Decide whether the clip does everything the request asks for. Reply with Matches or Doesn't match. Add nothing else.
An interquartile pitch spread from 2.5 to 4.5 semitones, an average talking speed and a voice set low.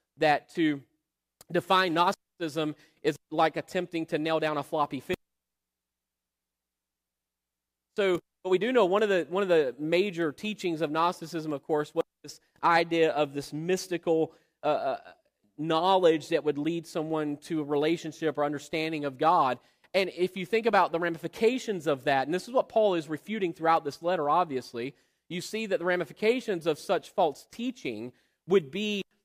Doesn't match